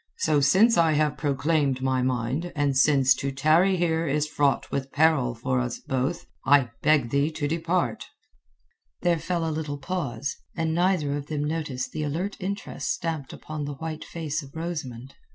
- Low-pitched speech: No, medium, 150 Hz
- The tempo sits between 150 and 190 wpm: Yes, average, 170 wpm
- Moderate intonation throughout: Yes, average, 3.2 semitones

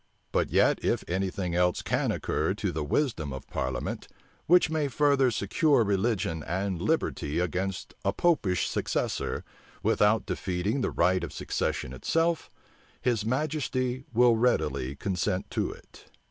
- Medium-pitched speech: No, low, 100 Hz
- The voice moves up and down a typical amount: No, wide, 6.4 semitones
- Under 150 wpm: Yes, average, 140 wpm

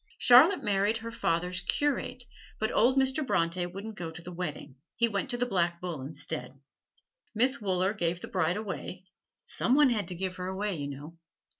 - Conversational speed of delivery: Yes, average, 185 wpm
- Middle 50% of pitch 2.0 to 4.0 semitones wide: No, average, 5.2 semitones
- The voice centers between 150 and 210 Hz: Yes, high, 190 Hz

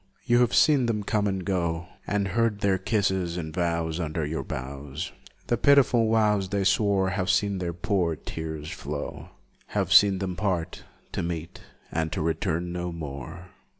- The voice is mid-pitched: No, very low, 90 Hz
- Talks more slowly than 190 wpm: Yes, average, 165 wpm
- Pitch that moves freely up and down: No, average, 3.7 semitones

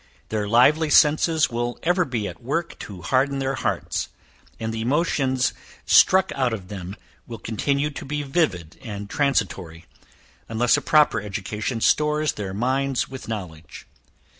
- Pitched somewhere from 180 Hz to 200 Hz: No, low, 125 Hz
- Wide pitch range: Yes, wide, 5.7 semitones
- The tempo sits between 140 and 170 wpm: Yes, average, 145 wpm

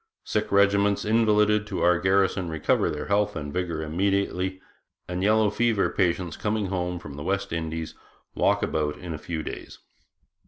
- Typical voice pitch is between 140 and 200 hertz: No, very low, 95 Hz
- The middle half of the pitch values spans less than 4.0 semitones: Yes, average, 3.5 semitones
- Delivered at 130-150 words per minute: No, average, 160 wpm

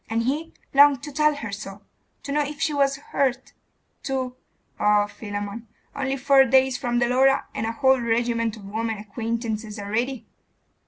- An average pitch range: Yes, average, 3.5 semitones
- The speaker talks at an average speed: Yes, average, 165 wpm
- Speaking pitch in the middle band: No, high, 240 Hz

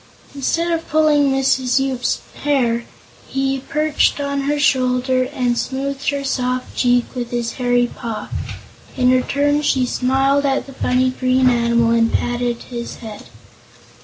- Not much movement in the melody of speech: Yes, narrow, 2.2 semitones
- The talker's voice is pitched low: No, very high, 255 Hz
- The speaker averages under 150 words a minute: Yes, average, 140 wpm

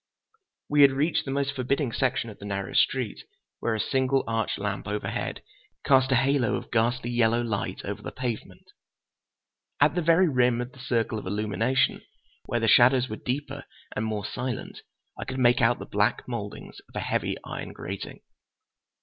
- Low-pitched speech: Yes, low, 120 Hz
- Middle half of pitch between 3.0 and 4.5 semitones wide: Yes, average, 3.3 semitones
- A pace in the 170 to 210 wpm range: Yes, average, 175 wpm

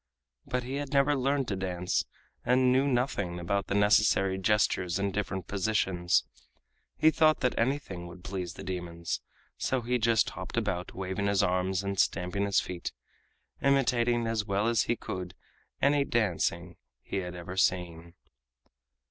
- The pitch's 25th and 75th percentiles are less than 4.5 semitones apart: No, average, 5.2 semitones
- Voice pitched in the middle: No, low, 100 Hz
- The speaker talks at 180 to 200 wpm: No, average, 155 wpm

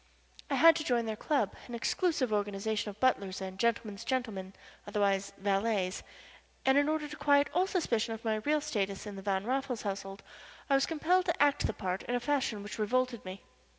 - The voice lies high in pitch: Yes, high, 225 Hz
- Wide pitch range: Yes, wide, 5.8 semitones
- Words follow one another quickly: No, average, 195 wpm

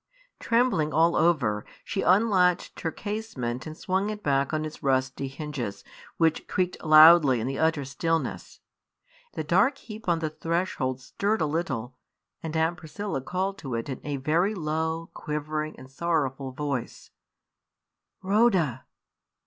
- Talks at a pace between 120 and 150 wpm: Yes, average, 140 wpm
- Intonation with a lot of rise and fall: No, average, 4.8 semitones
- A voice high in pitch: No, medium, 155 Hz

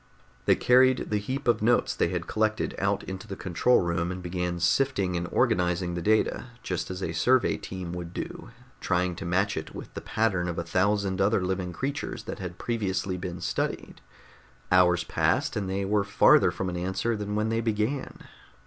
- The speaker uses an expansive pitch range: No, average, 3.3 semitones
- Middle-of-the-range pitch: No, very low, 95 Hz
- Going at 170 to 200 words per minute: Yes, average, 190 wpm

